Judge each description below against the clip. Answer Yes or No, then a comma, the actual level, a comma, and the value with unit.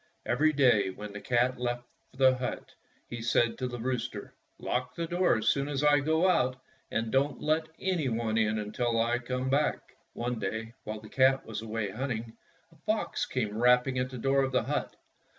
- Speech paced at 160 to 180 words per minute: No, average, 195 wpm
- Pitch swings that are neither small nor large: Yes, average, 3.0 semitones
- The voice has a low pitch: Yes, low, 125 Hz